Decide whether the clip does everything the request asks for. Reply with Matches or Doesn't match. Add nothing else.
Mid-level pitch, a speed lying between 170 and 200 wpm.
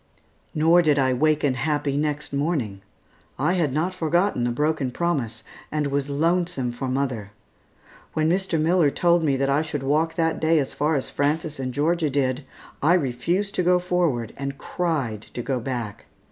Matches